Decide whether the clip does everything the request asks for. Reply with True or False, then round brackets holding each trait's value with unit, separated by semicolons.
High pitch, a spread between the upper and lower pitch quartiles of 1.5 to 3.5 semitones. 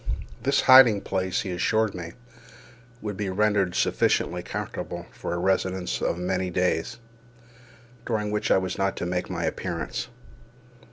False (95 Hz; 2.8 semitones)